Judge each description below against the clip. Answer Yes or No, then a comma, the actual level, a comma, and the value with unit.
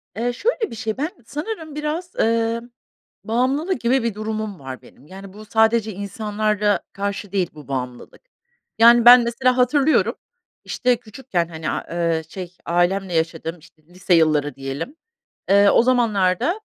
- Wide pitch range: Yes, wide, 5.8 semitones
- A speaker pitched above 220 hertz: No, high, 215 Hz